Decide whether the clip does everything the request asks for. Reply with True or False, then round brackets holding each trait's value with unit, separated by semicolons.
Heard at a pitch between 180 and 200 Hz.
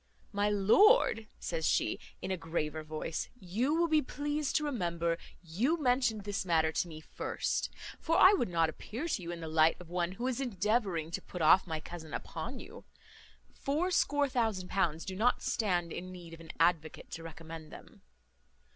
True (185 Hz)